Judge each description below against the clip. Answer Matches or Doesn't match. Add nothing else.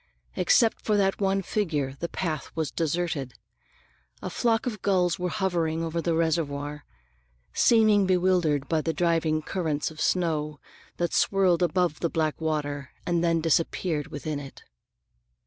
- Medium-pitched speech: Matches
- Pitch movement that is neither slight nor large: Matches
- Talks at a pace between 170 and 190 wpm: Doesn't match